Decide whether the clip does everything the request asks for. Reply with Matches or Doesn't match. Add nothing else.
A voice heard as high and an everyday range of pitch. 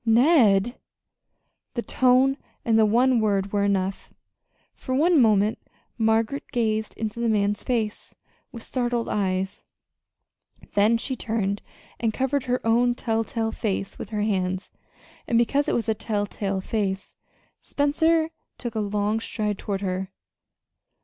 Matches